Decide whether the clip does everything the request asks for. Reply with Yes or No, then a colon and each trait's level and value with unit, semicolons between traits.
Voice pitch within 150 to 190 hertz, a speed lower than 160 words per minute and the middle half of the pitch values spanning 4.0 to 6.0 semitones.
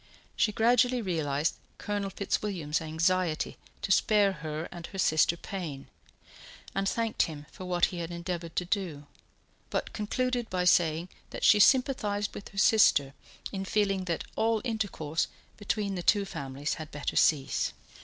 Yes: medium, 185 Hz; average, 150 wpm; average, 4.4 semitones